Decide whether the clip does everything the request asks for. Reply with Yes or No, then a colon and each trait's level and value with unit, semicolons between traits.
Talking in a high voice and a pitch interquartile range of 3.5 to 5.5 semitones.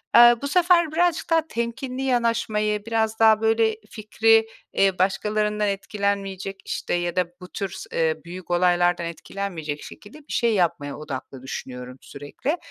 Yes: high, 210 Hz; average, 4.7 semitones